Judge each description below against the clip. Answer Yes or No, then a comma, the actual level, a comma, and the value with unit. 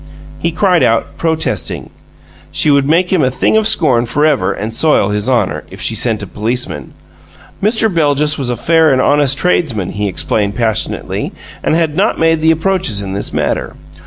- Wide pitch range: Yes, wide, 6.1 semitones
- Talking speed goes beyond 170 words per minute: Yes, average, 180 wpm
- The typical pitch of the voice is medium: Yes, medium, 145 Hz